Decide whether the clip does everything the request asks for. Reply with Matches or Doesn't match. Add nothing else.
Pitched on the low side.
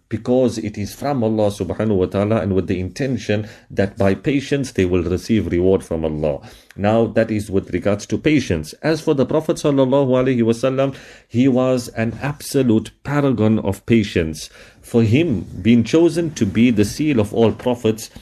Matches